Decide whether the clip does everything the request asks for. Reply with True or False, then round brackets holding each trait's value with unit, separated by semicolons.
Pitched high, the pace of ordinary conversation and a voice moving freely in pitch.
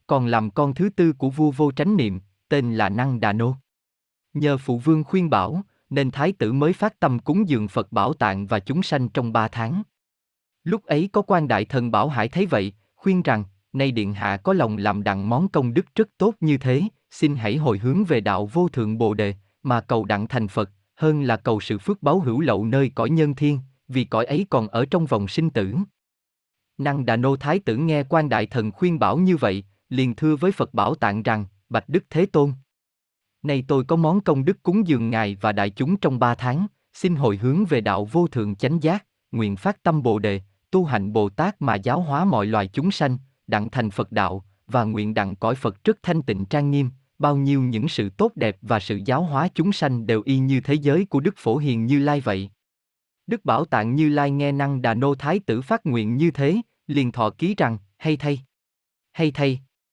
False (135 Hz; 225 wpm; 6.4 semitones)